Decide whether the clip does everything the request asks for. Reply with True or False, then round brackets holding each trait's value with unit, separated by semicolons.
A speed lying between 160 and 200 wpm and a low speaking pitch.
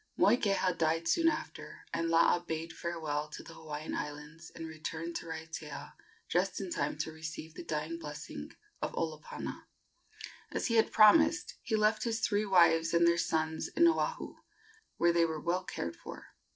False (165 wpm; 165 Hz)